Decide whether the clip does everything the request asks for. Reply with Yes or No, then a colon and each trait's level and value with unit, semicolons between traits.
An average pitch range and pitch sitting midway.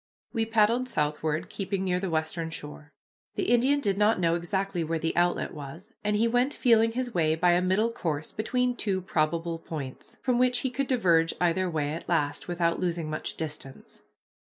No: wide, 5.8 semitones; medium, 180 Hz